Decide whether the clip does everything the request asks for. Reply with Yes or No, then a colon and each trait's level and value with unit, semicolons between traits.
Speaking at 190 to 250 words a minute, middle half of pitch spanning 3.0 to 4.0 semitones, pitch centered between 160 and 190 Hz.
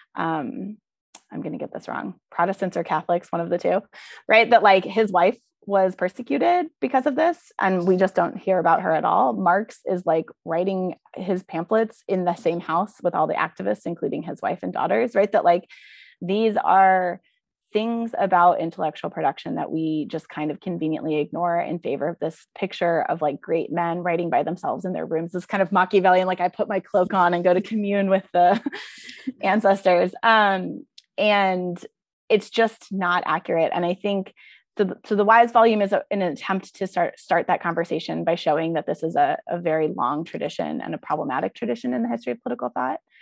Yes: average, 195 wpm; average, 3.3 semitones; medium, 185 Hz